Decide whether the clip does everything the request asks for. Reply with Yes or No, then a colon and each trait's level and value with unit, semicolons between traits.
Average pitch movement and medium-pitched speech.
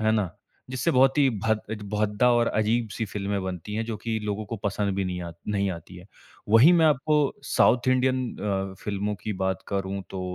No: average, 3.4 semitones; low, 105 Hz